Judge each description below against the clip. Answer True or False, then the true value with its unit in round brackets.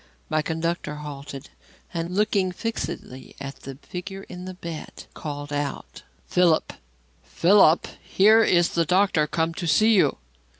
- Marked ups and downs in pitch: False (3.8 semitones)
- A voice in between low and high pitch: True (170 Hz)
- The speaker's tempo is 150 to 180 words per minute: False (135 wpm)